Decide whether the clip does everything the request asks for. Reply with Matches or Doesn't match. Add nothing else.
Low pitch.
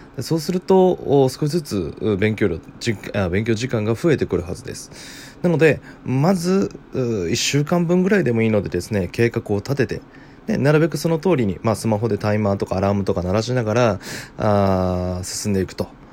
Matches